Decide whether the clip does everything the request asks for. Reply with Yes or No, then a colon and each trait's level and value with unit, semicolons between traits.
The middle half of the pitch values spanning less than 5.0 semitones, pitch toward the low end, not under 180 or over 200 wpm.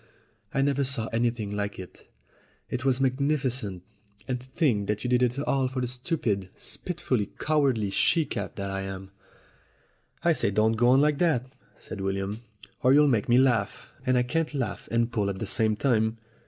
Yes: average, 4.5 semitones; low, 125 Hz; average, 185 wpm